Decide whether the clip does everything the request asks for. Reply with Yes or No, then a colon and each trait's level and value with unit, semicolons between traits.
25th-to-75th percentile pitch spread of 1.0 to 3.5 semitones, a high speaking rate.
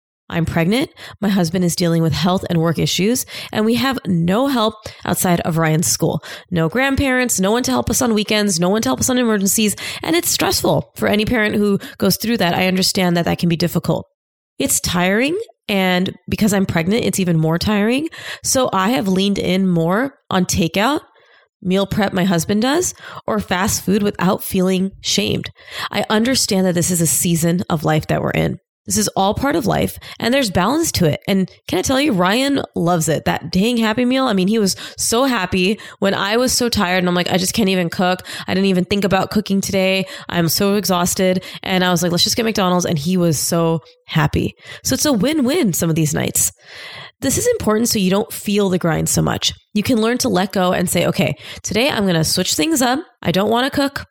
No: average, 4.2 semitones; fast, 220 wpm